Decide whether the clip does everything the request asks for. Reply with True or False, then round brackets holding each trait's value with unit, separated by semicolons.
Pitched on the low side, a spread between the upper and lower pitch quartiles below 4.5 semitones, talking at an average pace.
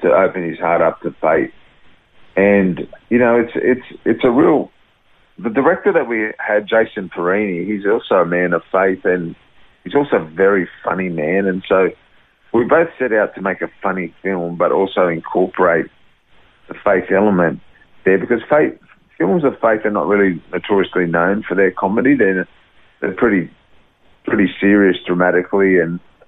True (95 Hz; 2.5 semitones; 165 wpm)